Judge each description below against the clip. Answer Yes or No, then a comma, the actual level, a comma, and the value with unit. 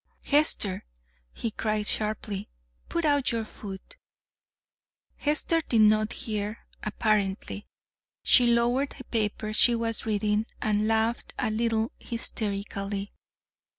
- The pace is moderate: No, slow, 110 wpm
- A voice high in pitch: Yes, high, 220 Hz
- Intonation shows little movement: Yes, narrow, 2.1 semitones